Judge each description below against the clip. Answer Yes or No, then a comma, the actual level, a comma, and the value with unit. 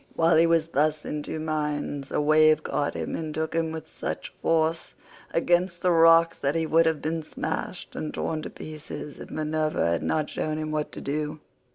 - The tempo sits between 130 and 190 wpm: No, average, 200 wpm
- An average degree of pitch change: No, narrow, 1.3 semitones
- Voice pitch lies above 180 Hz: No, medium, 155 Hz